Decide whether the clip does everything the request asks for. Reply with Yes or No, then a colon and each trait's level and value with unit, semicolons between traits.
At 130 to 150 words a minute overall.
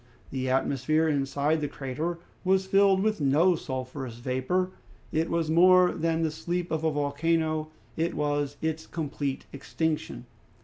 Yes: average, 140 wpm